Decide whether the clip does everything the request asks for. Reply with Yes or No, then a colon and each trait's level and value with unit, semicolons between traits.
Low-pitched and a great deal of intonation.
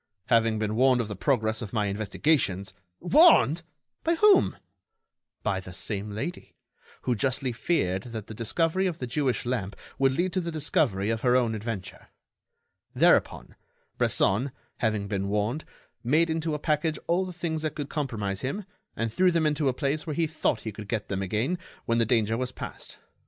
Yes: low, 125 Hz; wide, 6.6 semitones